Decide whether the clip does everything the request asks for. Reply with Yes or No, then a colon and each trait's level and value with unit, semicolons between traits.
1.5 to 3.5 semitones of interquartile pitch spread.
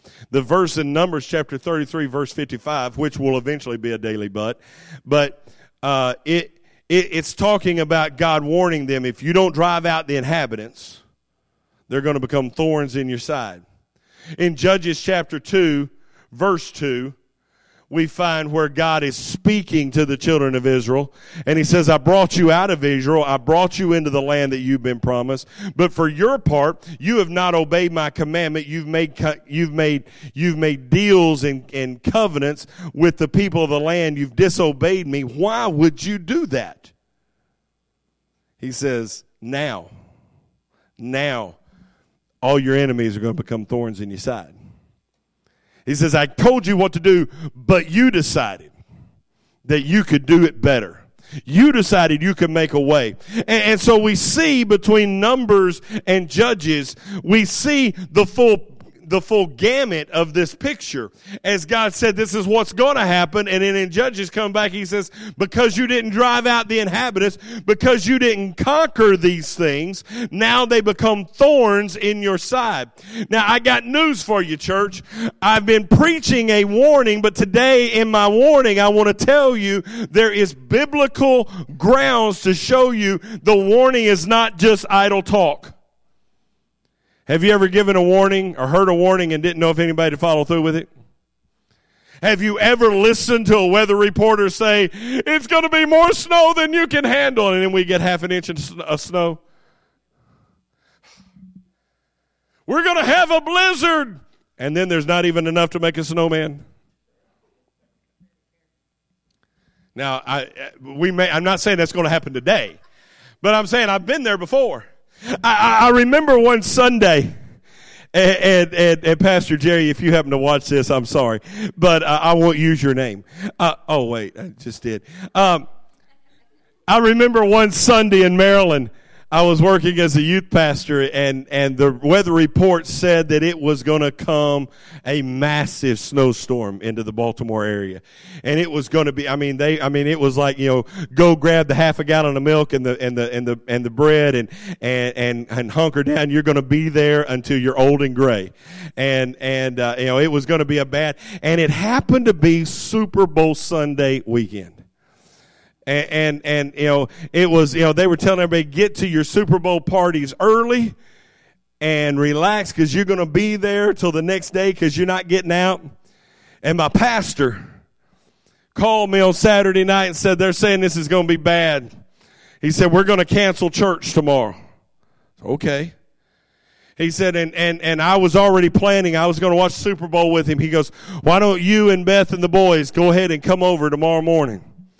No: wide, 5.5 semitones